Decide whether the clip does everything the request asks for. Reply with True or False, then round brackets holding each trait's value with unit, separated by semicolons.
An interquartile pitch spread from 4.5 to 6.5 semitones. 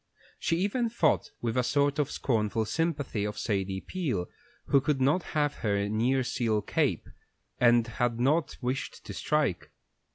True (5.3 semitones)